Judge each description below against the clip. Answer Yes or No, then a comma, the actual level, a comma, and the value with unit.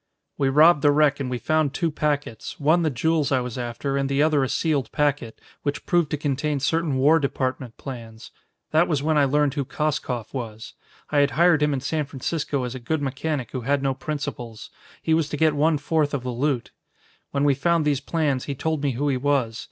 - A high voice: No, medium, 145 Hz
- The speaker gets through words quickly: Yes, fast, 220 wpm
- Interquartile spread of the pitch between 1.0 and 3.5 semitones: Yes, average, 2.7 semitones